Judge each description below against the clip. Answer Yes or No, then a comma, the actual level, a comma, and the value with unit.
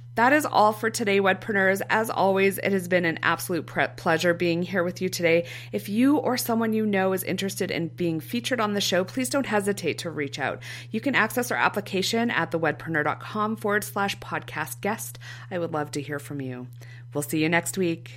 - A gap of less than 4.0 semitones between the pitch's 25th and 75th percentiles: No, wide, 5.6 semitones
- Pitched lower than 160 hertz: No, medium, 180 Hz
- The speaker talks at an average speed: No, fast, 210 wpm